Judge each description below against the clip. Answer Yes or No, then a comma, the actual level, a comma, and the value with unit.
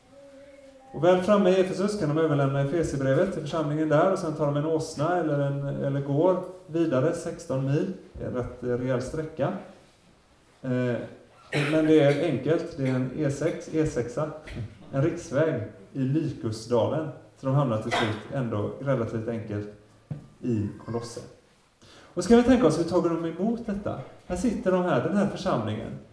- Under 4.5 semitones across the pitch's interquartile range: No, wide, 5.5 semitones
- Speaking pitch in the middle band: Yes, medium, 150 Hz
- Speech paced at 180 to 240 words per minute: No, average, 155 wpm